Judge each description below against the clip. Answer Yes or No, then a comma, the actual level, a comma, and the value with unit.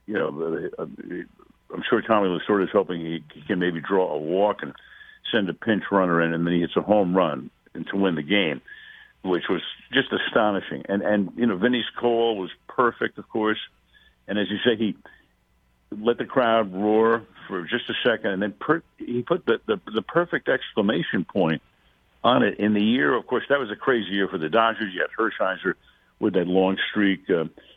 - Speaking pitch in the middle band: No, low, 105 Hz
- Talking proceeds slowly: No, average, 200 wpm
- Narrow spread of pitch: No, average, 3.7 semitones